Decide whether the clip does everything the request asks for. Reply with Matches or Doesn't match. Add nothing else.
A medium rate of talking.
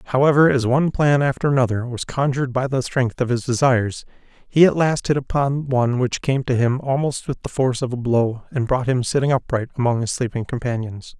Doesn't match